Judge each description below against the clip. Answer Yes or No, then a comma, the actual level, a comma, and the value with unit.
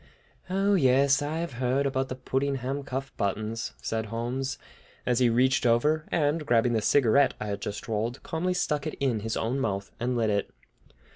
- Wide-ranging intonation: No, average, 3.6 semitones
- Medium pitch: No, low, 130 Hz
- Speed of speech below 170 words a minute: No, average, 185 wpm